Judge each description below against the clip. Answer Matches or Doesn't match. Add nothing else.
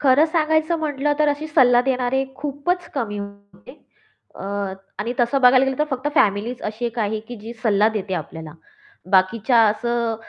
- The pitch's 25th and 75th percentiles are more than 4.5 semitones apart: Matches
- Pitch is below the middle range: Doesn't match